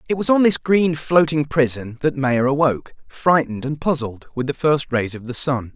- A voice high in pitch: No, medium, 140 Hz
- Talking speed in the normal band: No, fast, 210 wpm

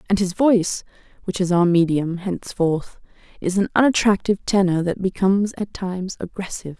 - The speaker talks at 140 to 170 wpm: Yes, average, 150 wpm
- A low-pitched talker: No, high, 190 Hz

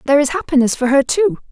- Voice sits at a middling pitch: No, very high, 280 Hz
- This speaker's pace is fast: Yes, fast, 235 wpm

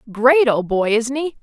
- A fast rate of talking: Yes, fast, 210 wpm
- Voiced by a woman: Yes, female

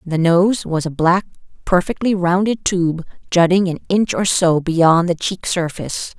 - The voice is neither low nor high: Yes, medium, 175 Hz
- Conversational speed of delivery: Yes, average, 165 wpm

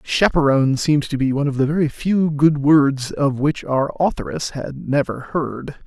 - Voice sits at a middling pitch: Yes, medium, 145 Hz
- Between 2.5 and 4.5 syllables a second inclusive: Yes, 4.4 syllables/s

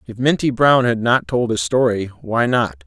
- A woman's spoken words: No, male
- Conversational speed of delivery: No, fast, 210 wpm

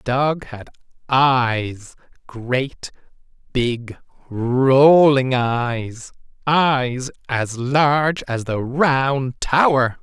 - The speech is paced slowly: Yes, slow, 90 wpm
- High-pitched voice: No, low, 130 Hz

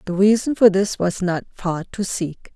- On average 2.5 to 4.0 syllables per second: No, 4.4 syllables/s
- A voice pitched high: Yes, high, 195 Hz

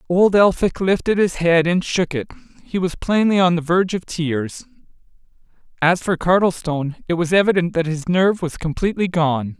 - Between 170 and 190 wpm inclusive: Yes, average, 175 wpm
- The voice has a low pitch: No, medium, 175 Hz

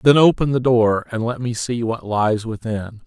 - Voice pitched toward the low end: Yes, low, 115 Hz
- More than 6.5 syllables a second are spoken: No, 4.5 syllables/s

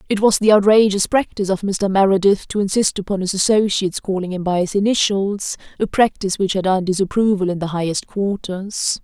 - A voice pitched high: Yes, high, 195 Hz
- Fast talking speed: No, average, 185 wpm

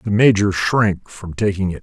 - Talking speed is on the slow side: No, average, 200 wpm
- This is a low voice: Yes, low, 100 Hz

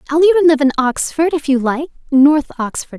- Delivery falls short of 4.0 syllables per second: No, 5.6 syllables/s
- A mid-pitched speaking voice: No, very high, 290 Hz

